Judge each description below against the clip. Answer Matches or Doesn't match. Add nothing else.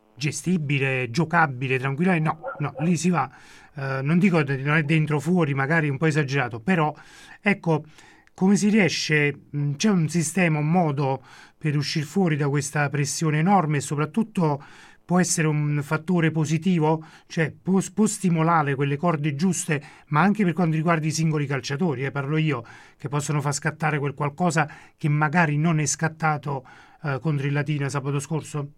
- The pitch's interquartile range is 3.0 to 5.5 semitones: Doesn't match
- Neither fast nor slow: Doesn't match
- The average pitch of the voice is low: Doesn't match